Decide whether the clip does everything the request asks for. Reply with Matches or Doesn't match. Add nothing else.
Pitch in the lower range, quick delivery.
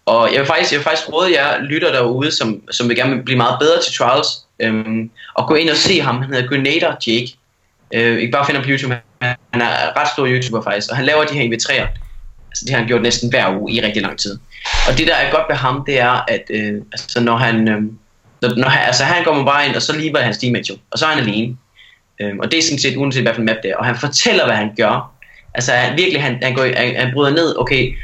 Matches